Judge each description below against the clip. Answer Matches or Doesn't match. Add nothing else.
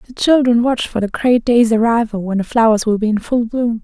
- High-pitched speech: Matches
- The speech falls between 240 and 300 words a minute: Matches